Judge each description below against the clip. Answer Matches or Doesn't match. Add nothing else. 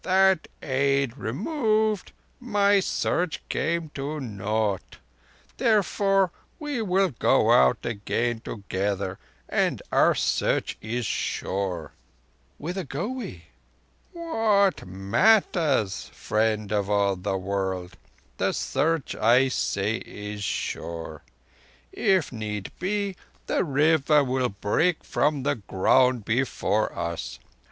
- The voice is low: Matches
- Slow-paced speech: Matches